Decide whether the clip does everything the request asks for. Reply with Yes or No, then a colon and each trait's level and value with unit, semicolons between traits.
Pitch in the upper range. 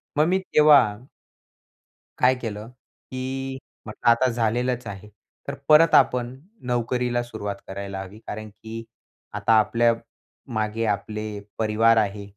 No: low, 115 Hz